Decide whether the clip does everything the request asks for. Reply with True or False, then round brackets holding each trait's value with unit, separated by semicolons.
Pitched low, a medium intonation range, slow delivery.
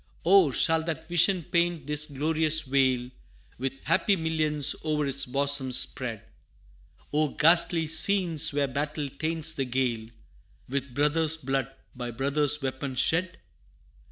False (150 Hz; 3.2 semitones; 130 wpm)